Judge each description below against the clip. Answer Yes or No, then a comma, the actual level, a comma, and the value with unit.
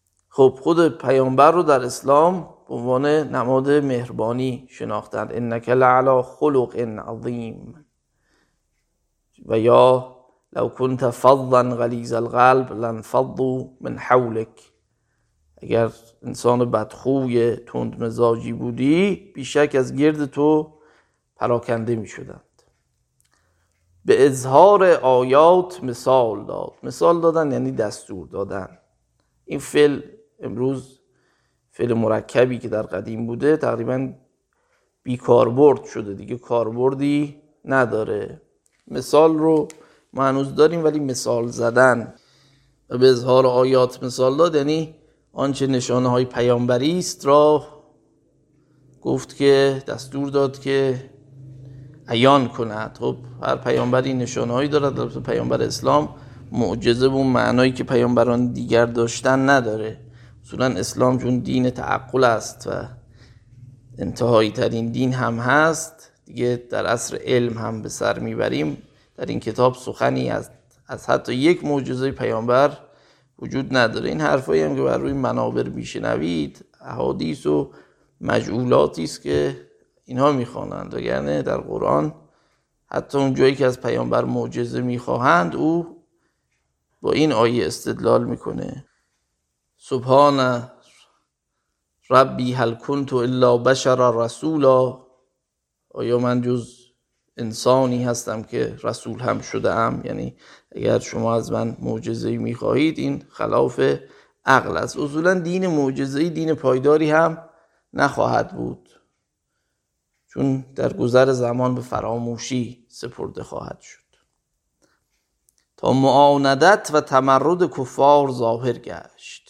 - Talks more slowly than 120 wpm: Yes, average, 110 wpm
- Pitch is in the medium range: No, low, 125 Hz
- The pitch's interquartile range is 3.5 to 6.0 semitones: No, average, 2.9 semitones